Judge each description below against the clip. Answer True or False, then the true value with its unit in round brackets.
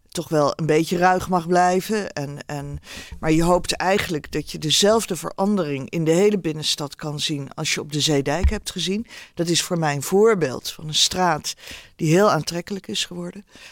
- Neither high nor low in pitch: True (175 Hz)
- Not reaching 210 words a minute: True (195 wpm)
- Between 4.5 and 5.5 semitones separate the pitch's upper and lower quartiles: False (4.0 semitones)